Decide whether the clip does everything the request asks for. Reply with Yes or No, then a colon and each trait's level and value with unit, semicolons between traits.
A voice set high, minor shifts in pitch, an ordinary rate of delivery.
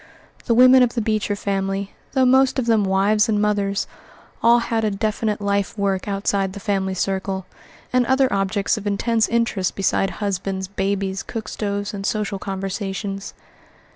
Yes: high, 200 Hz; narrow, 2.2 semitones; average, 160 wpm